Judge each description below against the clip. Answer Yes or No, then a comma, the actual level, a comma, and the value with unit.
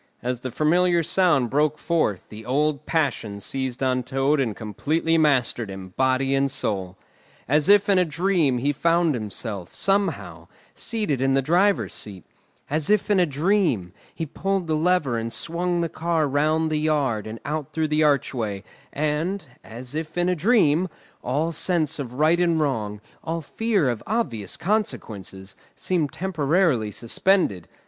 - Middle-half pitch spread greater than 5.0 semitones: Yes, wide, 5.6 semitones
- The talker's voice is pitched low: No, medium, 150 Hz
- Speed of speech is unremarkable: Yes, average, 160 wpm